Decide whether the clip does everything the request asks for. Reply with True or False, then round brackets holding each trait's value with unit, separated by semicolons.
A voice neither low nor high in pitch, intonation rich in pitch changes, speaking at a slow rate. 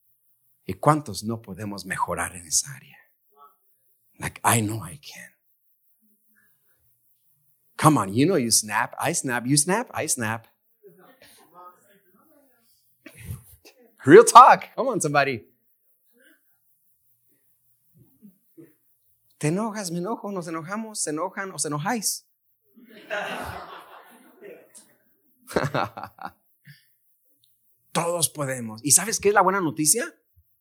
True (150 Hz; 8.8 semitones; 100 wpm)